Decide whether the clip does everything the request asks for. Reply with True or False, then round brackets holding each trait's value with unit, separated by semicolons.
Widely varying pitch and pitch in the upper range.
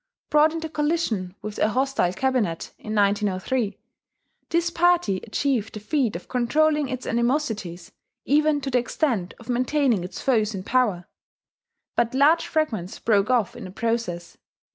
True (6.3 semitones; 240 Hz)